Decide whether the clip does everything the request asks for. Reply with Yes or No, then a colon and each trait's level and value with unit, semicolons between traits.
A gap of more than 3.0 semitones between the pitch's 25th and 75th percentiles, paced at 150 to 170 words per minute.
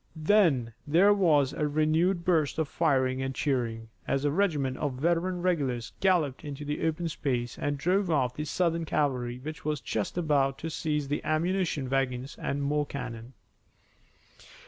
Yes: average, 3.8 semitones; average, 160 wpm